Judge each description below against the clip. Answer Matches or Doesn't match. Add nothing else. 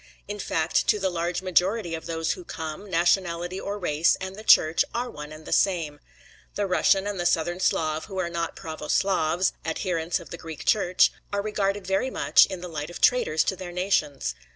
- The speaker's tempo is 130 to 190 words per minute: Doesn't match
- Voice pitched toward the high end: Doesn't match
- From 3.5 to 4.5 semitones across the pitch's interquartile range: Doesn't match